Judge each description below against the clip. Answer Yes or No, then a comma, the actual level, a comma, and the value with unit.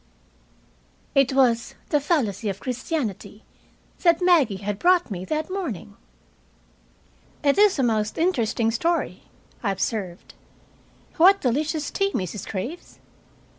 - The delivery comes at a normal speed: No, slow, 115 wpm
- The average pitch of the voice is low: No, very high, 260 Hz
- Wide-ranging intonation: Yes, wide, 7.9 semitones